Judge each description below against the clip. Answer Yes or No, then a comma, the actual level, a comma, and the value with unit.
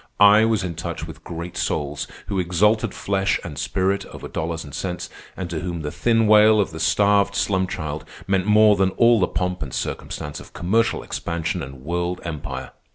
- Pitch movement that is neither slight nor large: Yes, average, 3.8 semitones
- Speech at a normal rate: Yes, average, 190 wpm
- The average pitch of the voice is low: Yes, very low, 90 Hz